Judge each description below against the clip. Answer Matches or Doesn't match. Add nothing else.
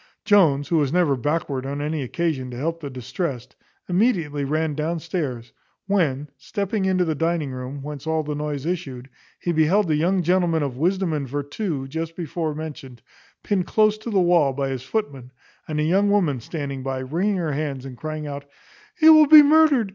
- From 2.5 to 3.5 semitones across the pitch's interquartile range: Doesn't match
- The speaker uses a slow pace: Doesn't match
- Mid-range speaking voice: Matches